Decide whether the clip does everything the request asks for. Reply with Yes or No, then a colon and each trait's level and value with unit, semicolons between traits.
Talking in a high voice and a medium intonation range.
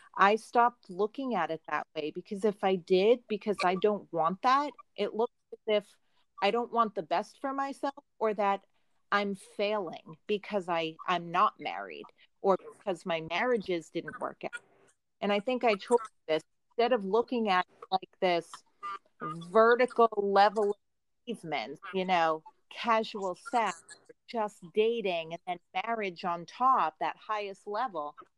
Yes: high, 205 Hz; average, 4.5 semitones